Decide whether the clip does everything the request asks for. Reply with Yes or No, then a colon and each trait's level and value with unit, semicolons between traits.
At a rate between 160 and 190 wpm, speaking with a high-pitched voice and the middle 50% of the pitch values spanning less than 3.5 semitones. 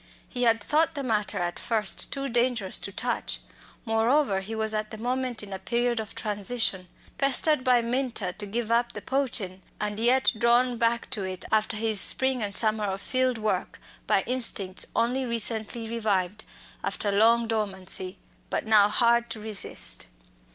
Yes: average, 165 wpm; high, 225 Hz; average, 2.8 semitones